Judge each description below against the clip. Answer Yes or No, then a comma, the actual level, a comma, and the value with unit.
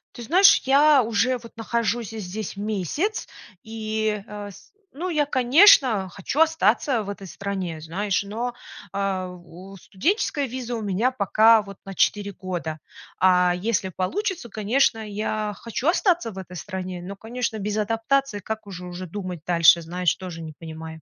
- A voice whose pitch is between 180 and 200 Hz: No, high, 210 Hz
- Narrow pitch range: No, average, 4.4 semitones